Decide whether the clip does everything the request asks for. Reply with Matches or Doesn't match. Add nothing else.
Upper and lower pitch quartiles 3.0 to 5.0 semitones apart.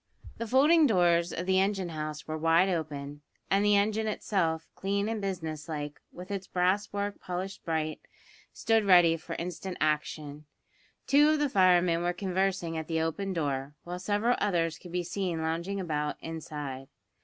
Matches